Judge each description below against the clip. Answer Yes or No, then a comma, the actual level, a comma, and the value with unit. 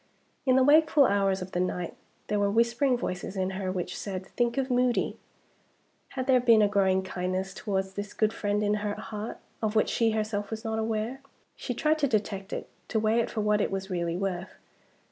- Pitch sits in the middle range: No, high, 210 Hz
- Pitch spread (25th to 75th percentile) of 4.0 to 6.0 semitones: No, average, 3.5 semitones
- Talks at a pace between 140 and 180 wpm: No, fast, 205 wpm